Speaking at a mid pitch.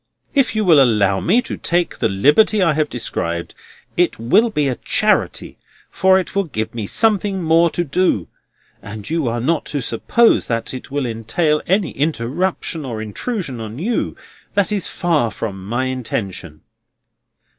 Yes: medium, 145 Hz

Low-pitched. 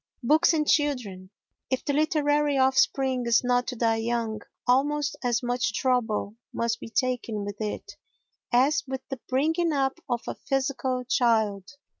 No: very high, 255 Hz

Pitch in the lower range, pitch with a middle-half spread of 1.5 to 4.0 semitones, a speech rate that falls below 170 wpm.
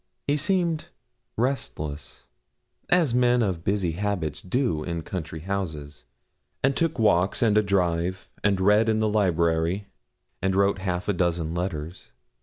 No: very low, 95 Hz; average, 4.5 semitones; average, 140 wpm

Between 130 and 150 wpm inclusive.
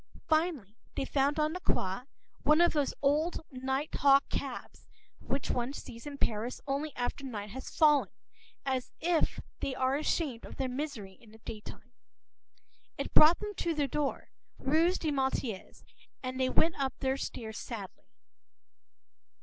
No: average, 160 wpm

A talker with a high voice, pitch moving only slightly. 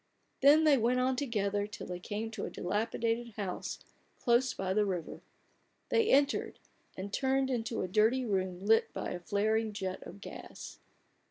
No: high, 220 Hz; average, 4.1 semitones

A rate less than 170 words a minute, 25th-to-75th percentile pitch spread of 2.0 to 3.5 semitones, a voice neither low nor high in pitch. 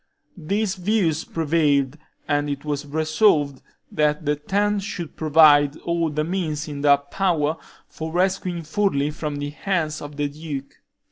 Yes: average, 145 wpm; average, 2.9 semitones; medium, 155 Hz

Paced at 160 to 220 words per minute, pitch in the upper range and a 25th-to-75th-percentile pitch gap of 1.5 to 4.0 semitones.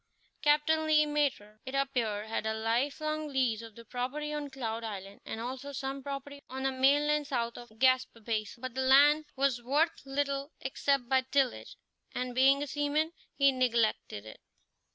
Yes: average, 175 wpm; very high, 265 Hz; average, 3.3 semitones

